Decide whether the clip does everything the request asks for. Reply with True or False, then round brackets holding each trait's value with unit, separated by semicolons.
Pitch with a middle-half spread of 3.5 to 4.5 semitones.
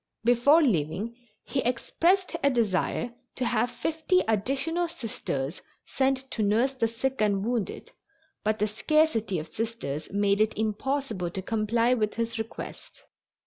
True (4.1 semitones)